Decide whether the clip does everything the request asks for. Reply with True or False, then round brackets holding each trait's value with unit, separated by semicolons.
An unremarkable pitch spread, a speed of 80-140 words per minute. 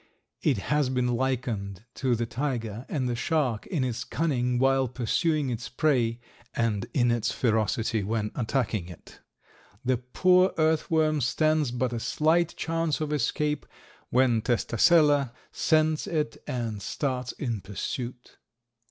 True (4.5 semitones; 135 wpm)